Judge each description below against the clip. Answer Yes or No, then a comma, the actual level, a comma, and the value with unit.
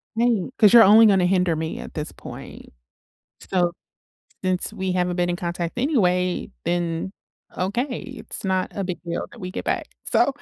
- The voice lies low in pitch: No, medium, 185 Hz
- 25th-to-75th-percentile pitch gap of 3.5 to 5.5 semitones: No, average, 2.9 semitones